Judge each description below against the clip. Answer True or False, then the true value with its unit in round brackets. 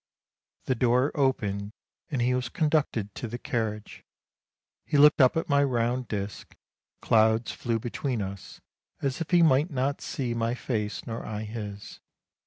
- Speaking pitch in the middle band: False (120 Hz)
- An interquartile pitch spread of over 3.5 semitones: True (3.9 semitones)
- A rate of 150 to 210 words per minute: True (160 wpm)